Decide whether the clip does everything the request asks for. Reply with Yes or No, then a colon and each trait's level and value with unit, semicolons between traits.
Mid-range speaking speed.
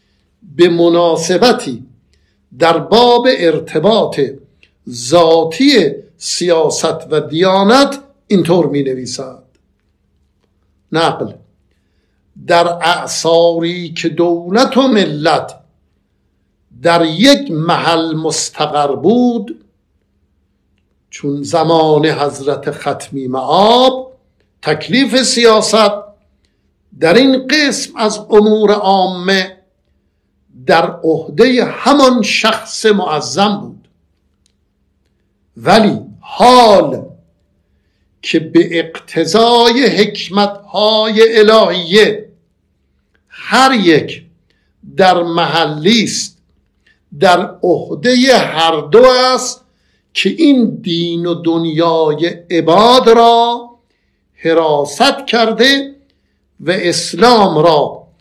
No: slow, 75 wpm